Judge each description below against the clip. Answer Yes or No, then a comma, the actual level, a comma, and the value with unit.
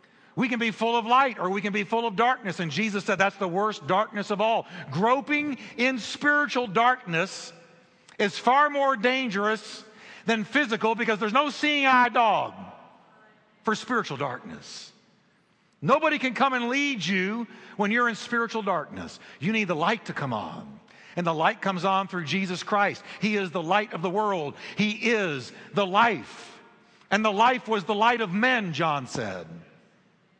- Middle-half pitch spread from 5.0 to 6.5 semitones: No, average, 3.7 semitones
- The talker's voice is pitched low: No, high, 215 Hz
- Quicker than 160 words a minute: Yes, average, 175 wpm